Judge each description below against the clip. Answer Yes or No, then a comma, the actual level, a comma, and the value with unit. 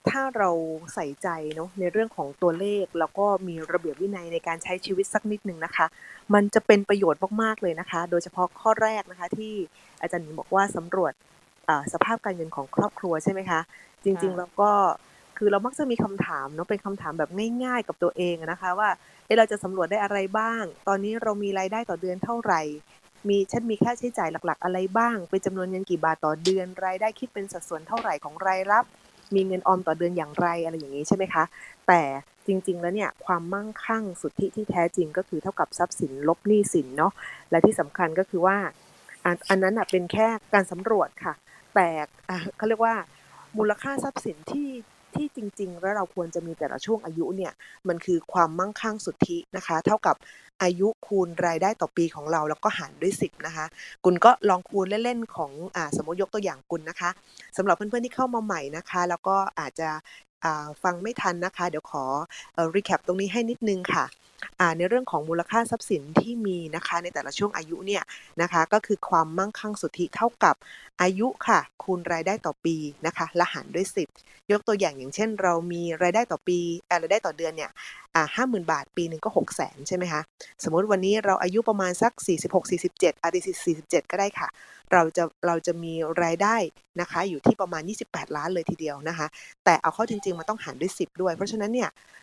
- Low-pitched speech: No, medium, 185 Hz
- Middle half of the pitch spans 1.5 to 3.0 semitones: No, average, 3.6 semitones